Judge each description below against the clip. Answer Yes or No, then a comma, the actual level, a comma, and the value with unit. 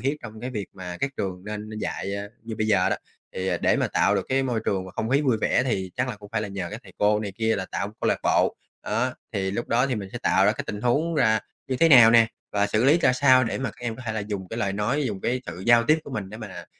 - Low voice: Yes, low, 110 Hz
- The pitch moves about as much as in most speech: Yes, average, 3.9 semitones